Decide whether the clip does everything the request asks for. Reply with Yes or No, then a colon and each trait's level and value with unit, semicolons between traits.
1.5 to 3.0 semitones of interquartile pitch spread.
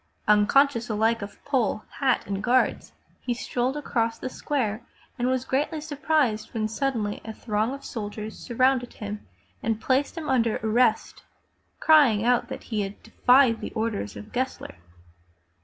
No: average, 3.5 semitones